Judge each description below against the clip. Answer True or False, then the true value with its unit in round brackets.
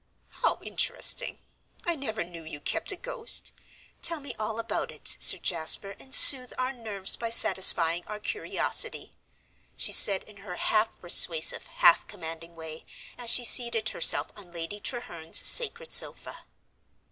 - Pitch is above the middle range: True (215 Hz)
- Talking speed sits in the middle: True (145 wpm)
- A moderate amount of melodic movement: False (6.9 semitones)